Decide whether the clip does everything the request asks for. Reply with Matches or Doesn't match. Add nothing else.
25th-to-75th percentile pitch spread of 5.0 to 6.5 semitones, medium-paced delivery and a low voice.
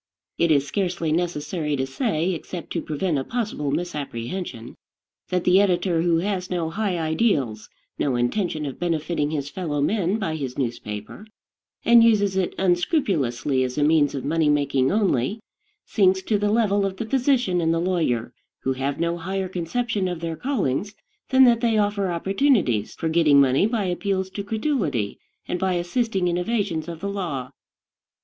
Doesn't match